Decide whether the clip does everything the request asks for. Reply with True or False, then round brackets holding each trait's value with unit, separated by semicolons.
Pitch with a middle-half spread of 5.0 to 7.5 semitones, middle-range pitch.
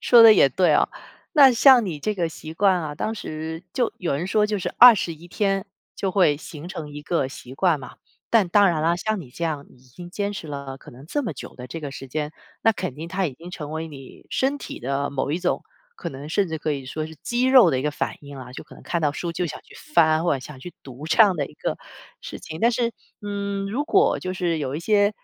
True (5.5 semitones; 165 Hz)